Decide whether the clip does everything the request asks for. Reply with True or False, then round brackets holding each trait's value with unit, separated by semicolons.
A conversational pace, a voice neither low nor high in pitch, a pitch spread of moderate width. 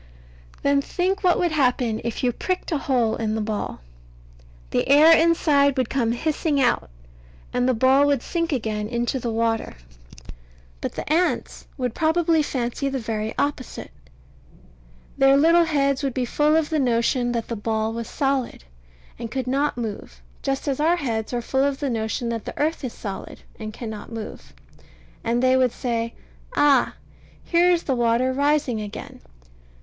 False (170 wpm; 260 Hz; 4.1 semitones)